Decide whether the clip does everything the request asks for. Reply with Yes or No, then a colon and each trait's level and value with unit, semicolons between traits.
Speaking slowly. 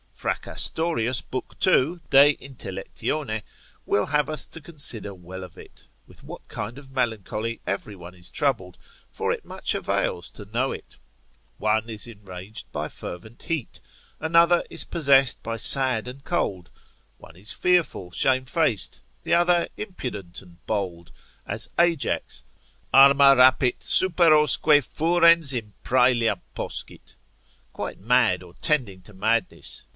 Yes: slow, 130 wpm